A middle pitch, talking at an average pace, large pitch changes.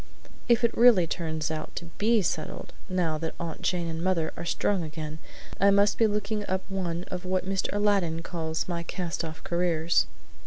No: medium, 180 Hz; average, 185 wpm; average, 3.2 semitones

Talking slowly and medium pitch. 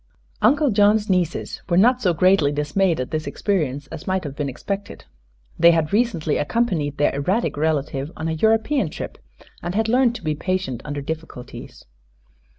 No: average, 165 wpm; medium, 170 Hz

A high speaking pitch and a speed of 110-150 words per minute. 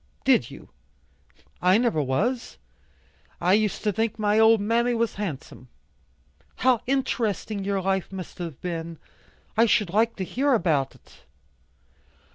Yes: high, 210 Hz; slow, 135 wpm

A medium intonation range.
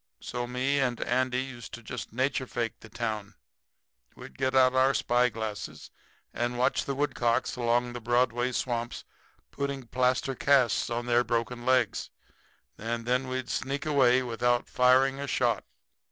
No: narrow, 1.5 semitones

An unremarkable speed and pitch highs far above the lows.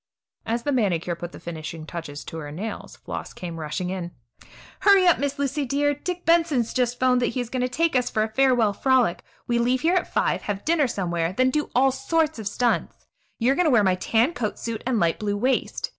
No: fast, 235 wpm; wide, 6.6 semitones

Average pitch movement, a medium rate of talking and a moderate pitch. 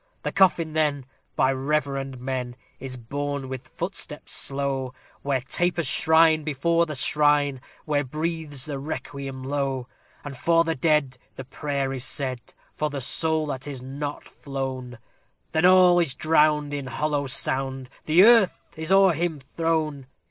Yes: average, 3.0 semitones; average, 150 wpm; medium, 145 Hz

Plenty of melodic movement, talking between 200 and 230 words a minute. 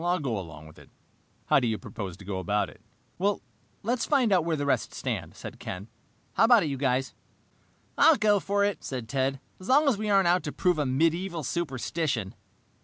Yes: wide, 8.3 semitones; fast, 205 wpm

